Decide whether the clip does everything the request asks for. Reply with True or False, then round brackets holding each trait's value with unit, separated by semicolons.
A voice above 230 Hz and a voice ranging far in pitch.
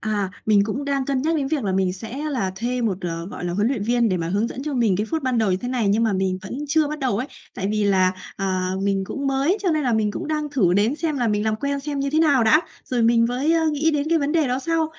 True (240 Hz; 6.0 semitones)